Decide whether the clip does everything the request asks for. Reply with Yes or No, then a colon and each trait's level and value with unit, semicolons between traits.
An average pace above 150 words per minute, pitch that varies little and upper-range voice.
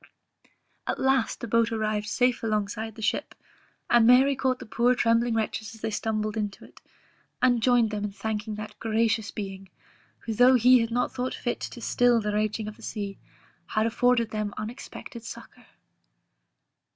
Yes: average, 175 wpm; narrow, 2.3 semitones; high, 225 Hz